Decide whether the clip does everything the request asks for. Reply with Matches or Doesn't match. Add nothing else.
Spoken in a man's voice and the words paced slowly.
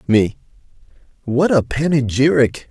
Matches